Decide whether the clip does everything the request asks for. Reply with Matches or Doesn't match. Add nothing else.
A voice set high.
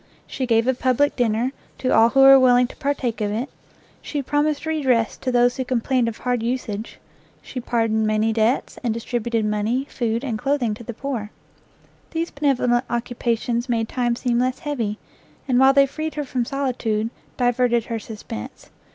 Matches